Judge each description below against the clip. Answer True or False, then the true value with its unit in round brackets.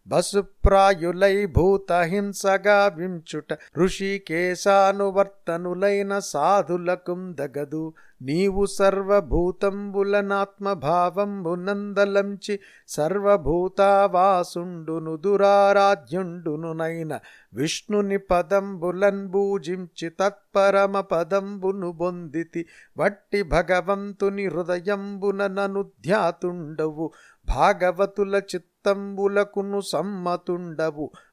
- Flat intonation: True (2.3 semitones)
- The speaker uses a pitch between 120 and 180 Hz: False (195 Hz)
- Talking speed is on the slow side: True (50 wpm)